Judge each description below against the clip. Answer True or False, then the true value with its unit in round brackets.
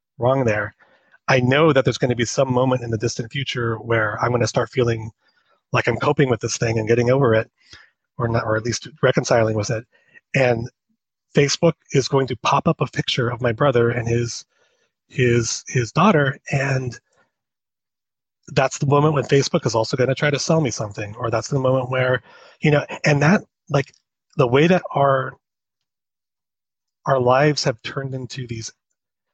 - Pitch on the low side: True (130 Hz)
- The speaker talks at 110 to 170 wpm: False (185 wpm)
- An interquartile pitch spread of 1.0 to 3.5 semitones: True (3.2 semitones)